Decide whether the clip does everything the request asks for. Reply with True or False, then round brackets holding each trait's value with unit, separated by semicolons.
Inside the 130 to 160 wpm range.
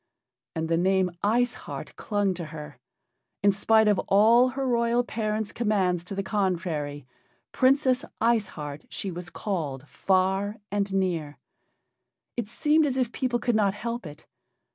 True (150 wpm)